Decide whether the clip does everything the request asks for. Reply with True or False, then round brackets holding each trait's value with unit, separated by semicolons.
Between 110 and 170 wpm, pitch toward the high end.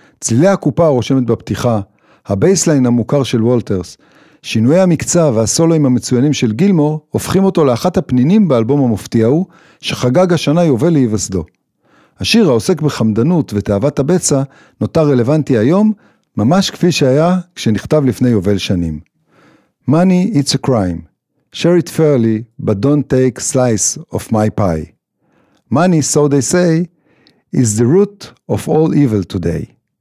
False (130 wpm; 140 Hz)